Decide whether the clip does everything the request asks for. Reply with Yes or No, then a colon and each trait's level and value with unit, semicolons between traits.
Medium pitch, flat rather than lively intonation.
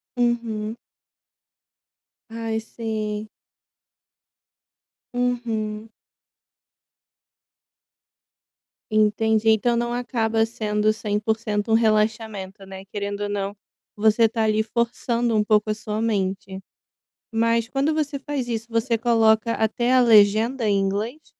No: high, 220 Hz; narrow, 1.7 semitones